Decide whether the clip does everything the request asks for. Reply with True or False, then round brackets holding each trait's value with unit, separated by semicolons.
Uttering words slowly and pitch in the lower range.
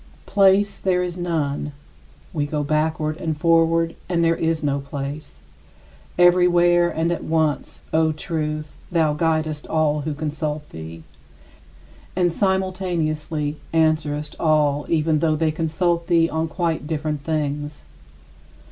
False (125 wpm; 155 Hz)